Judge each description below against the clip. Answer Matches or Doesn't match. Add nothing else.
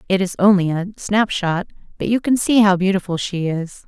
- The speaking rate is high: Matches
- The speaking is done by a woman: Matches